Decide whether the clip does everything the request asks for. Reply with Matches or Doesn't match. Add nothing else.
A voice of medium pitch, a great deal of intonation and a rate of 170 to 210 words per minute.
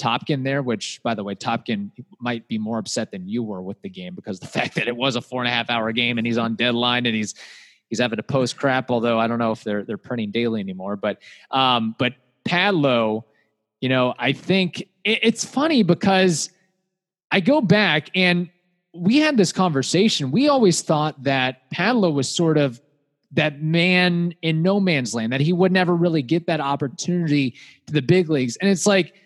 Matches